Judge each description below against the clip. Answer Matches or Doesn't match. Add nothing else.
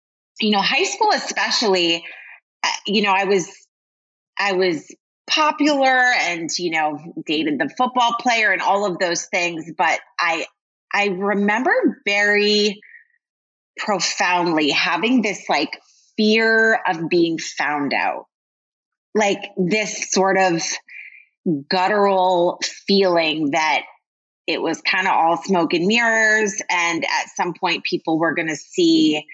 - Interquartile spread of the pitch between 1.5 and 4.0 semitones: Doesn't match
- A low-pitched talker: Doesn't match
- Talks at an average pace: Doesn't match